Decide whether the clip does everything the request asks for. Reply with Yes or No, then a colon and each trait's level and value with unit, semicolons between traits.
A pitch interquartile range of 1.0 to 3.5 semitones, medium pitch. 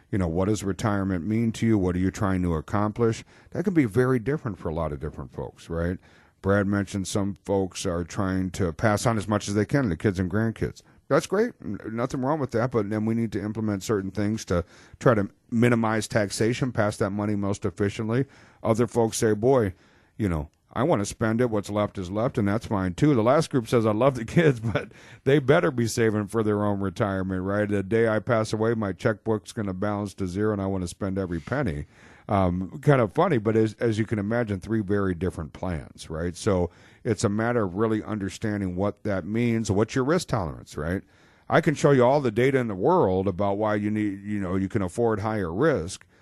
No: average, 3.0 semitones; low, 105 Hz